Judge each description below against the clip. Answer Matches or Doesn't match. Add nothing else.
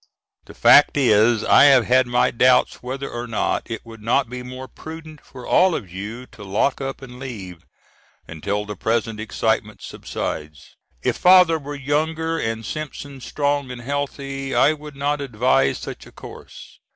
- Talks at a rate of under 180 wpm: Matches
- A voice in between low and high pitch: Doesn't match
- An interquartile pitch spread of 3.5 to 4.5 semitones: Matches